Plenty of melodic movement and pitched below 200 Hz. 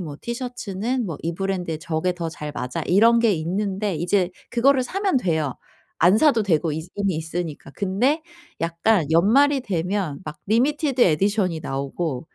Yes: wide, 6.2 semitones; high, 190 Hz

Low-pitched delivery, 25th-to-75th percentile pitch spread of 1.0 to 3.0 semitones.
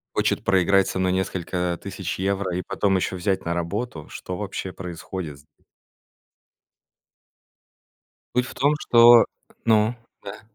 Yes: very low, 95 Hz; narrow, 2.4 semitones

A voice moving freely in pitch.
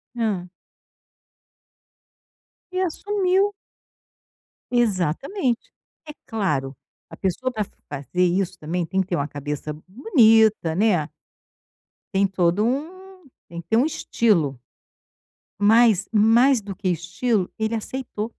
Yes: wide, 6.0 semitones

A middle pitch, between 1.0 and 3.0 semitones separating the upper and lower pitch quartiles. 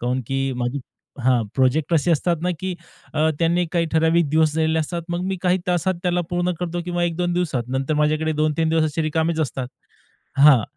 Yes: medium, 160 Hz; average, 2.7 semitones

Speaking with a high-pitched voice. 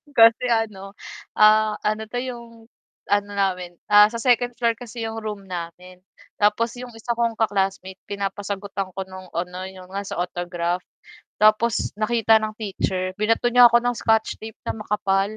Yes: high, 210 Hz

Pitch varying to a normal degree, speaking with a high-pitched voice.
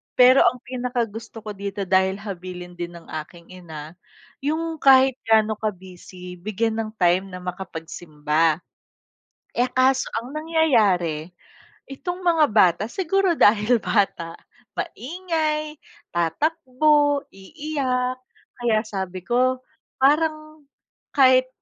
No: wide, 7.3 semitones; high, 225 Hz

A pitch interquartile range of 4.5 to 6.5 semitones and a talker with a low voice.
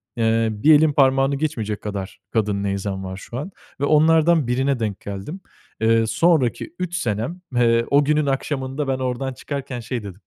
Yes: average, 5.0 semitones; low, 130 Hz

